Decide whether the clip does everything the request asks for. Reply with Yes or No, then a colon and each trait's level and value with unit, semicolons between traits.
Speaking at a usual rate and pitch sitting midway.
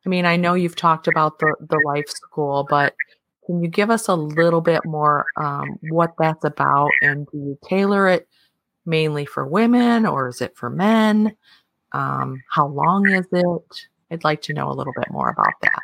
Yes: average, 195 wpm; medium, 165 Hz